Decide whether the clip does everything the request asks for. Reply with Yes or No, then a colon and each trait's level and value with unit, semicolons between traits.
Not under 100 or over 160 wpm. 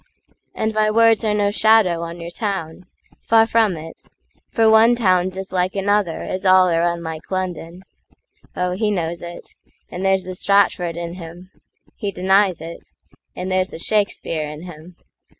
Yes: average, 150 wpm